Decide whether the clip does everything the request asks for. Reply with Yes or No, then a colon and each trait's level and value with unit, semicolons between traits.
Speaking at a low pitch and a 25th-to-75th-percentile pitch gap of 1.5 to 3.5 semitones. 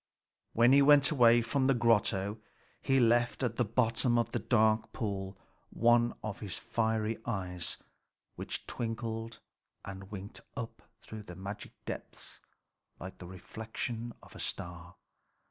Yes: low, 110 Hz; average, 3.1 semitones